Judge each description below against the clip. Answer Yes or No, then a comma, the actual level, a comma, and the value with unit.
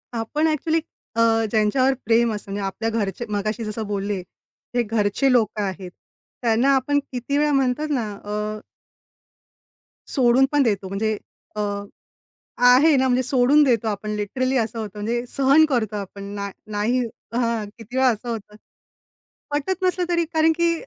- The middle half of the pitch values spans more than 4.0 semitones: Yes, average, 4.5 semitones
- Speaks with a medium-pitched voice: No, high, 235 Hz